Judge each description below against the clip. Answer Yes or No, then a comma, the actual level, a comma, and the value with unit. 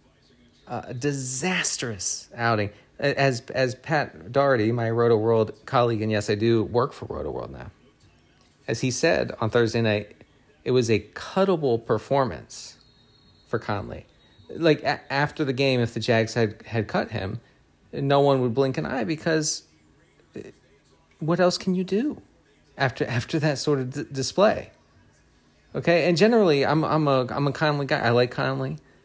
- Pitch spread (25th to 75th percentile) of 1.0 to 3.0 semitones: No, average, 4.3 semitones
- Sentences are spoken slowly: No, average, 160 wpm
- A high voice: No, low, 130 Hz